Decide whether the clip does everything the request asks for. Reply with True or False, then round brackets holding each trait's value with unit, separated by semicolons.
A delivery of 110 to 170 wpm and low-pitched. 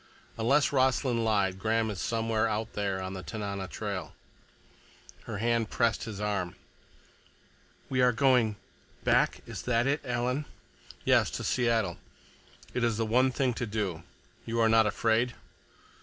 True (140 wpm; 115 Hz)